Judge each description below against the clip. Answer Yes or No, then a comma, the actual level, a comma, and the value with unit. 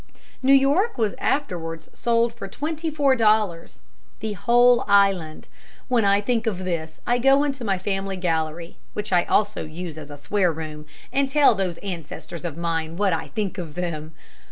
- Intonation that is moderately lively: No, wide, 6.3 semitones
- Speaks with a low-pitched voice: No, high, 195 Hz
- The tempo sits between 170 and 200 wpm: Yes, average, 175 wpm